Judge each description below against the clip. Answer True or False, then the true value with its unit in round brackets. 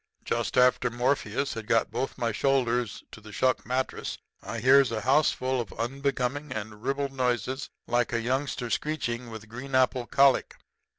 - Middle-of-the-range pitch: False (125 Hz)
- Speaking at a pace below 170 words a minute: True (160 wpm)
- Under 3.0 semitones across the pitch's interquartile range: True (2.6 semitones)